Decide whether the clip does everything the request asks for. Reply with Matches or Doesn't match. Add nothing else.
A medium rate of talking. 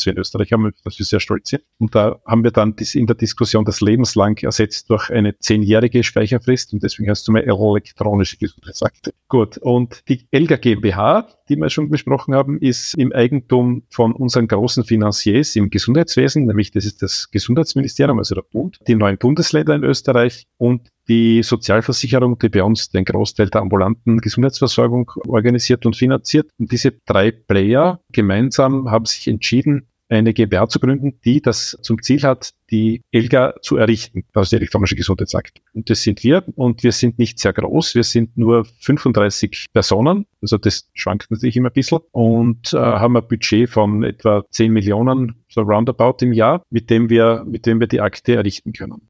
Matches